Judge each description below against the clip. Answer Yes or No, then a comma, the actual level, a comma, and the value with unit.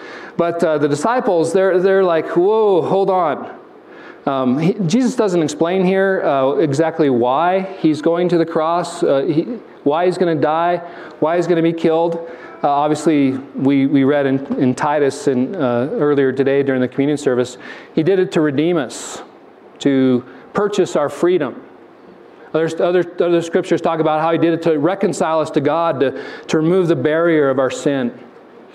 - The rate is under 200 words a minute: Yes, average, 180 wpm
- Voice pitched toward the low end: No, medium, 165 Hz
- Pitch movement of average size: Yes, average, 3.7 semitones